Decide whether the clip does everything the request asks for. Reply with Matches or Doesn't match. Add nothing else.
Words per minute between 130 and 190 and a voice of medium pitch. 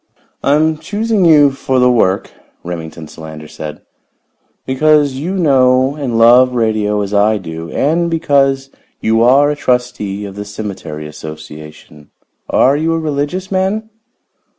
Doesn't match